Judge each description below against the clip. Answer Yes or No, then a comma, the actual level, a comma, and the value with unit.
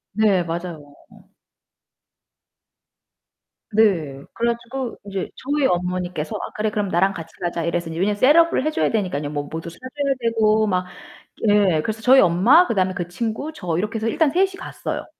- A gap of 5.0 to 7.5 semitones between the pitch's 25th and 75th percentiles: Yes, wide, 5.4 semitones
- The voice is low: No, high, 200 Hz